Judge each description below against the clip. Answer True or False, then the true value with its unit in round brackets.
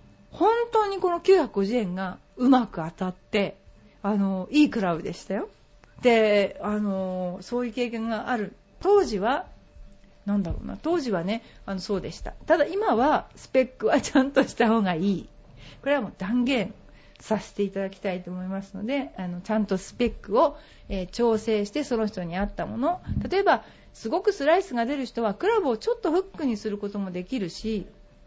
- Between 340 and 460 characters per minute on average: False (315 characters per minute)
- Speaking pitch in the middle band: False (220 Hz)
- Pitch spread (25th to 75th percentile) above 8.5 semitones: False (6.1 semitones)